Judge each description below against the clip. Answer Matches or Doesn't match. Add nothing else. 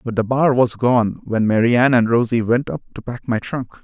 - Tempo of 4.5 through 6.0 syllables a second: Matches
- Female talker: Doesn't match